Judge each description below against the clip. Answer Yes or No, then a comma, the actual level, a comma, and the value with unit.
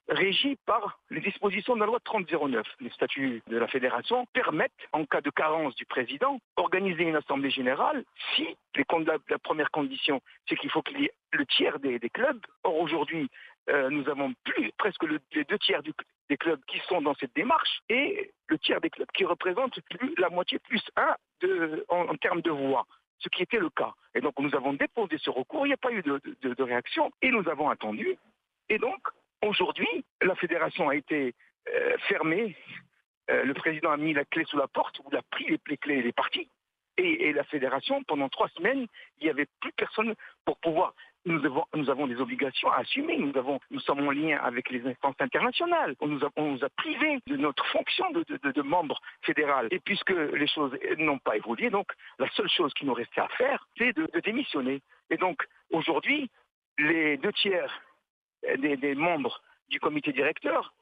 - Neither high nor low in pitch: No, high, 220 Hz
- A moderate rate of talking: No, fast, 205 wpm